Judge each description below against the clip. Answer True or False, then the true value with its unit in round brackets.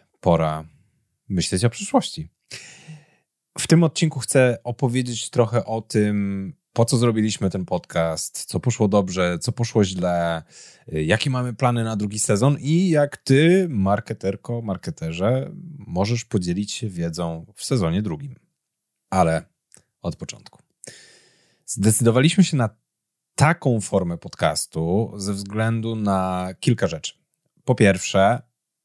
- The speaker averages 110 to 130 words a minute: True (120 wpm)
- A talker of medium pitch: False (110 Hz)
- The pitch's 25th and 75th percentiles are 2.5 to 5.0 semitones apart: False (5.4 semitones)